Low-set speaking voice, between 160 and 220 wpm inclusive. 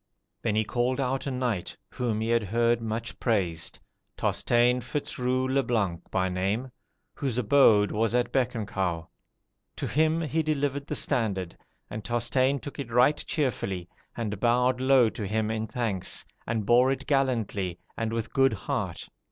Yes: low, 120 Hz; average, 165 wpm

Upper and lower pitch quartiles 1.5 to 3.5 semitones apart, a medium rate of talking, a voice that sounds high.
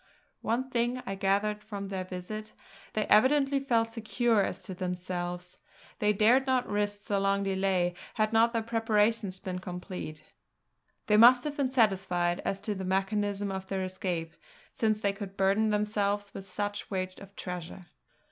Yes: average, 2.8 semitones; average, 165 wpm; high, 205 Hz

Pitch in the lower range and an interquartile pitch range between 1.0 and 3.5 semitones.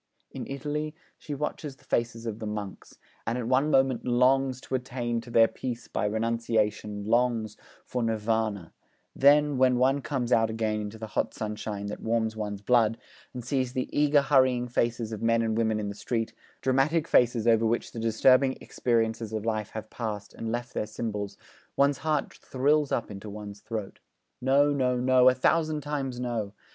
Yes: low, 115 Hz; average, 3.0 semitones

